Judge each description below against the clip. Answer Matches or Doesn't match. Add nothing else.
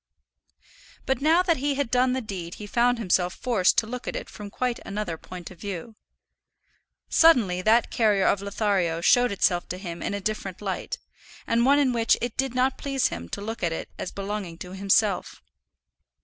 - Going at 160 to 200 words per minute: Matches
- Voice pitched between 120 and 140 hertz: Doesn't match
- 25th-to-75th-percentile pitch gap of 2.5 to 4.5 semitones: Doesn't match